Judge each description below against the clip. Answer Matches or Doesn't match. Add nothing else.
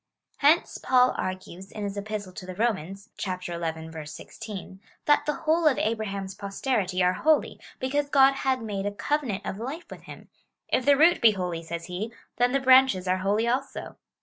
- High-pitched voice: Matches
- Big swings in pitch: Matches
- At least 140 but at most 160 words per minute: Doesn't match